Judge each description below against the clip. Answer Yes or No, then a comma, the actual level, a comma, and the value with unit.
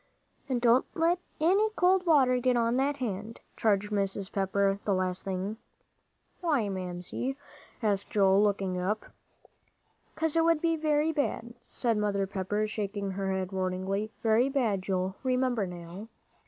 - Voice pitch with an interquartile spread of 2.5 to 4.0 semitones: No, average, 5.2 semitones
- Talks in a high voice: Yes, high, 210 Hz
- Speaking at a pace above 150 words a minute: No, average, 145 wpm